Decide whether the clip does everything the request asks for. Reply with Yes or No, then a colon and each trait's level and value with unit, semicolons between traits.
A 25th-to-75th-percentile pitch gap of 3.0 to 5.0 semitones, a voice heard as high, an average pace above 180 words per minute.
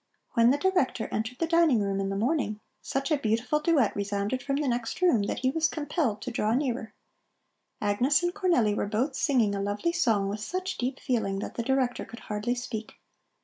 No: wide, 5.6 semitones; high, 245 Hz; average, 200 wpm